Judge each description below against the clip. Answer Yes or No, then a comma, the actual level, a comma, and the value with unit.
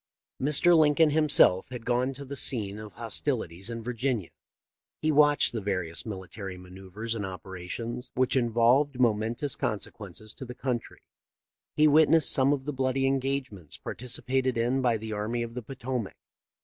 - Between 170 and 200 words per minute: No, average, 155 wpm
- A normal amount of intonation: Yes, average, 4.0 semitones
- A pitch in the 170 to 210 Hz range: No, low, 120 Hz